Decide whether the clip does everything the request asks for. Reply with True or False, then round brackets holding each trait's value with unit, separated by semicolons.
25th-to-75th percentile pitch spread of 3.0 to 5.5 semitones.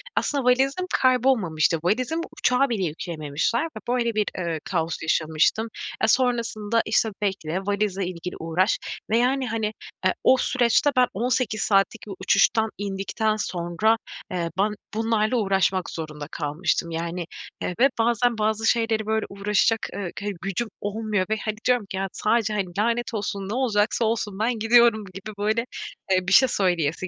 True (3.8 semitones)